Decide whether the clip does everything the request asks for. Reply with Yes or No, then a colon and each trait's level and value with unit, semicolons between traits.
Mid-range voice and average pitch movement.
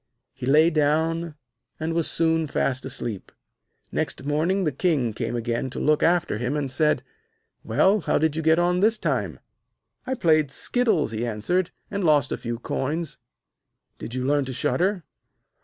Yes: medium, 155 Hz; average, 4.4 semitones